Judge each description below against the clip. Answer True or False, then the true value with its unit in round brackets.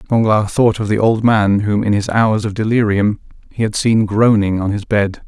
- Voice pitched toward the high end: False (105 Hz)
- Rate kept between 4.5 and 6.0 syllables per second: True (4.7 syllables/s)